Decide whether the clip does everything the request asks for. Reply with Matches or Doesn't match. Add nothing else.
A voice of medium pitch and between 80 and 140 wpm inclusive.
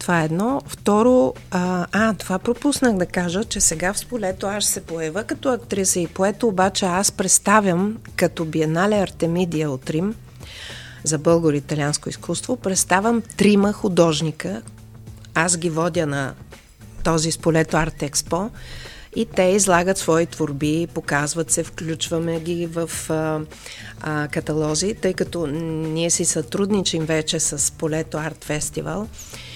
Matches